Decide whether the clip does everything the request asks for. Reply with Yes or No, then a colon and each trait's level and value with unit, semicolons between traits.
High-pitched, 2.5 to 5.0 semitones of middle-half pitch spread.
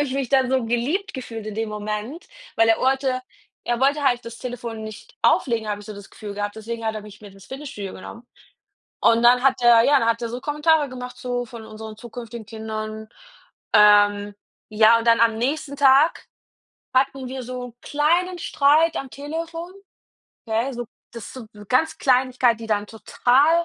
Yes: high, 240 Hz; average, 3.6 semitones